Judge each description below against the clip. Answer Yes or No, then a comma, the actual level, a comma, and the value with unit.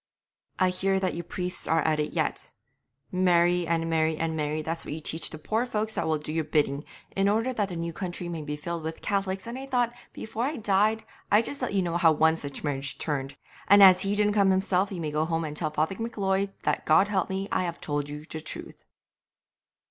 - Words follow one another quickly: Yes, fast, 230 wpm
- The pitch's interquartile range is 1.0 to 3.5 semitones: No, average, 3.9 semitones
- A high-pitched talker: No, medium, 175 Hz